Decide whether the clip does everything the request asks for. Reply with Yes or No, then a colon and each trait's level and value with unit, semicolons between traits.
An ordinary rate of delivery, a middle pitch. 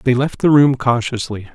No: average, 195 wpm; low, 125 Hz